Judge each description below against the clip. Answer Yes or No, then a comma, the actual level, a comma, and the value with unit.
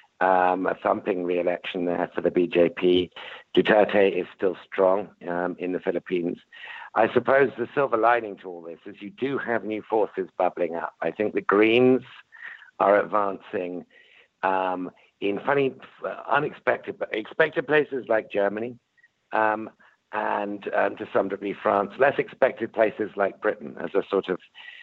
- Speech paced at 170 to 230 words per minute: No, average, 150 wpm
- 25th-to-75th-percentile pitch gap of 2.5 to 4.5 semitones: No, average, 5.2 semitones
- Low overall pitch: Yes, low, 105 Hz